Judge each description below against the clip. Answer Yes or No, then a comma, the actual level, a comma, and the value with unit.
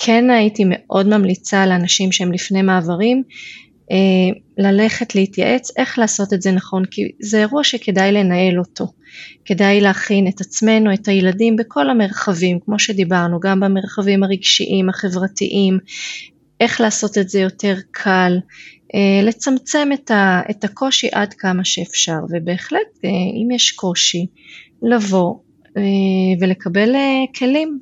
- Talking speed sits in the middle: Yes, average, 120 wpm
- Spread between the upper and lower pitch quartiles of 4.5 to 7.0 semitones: No, average, 3.3 semitones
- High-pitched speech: Yes, high, 200 Hz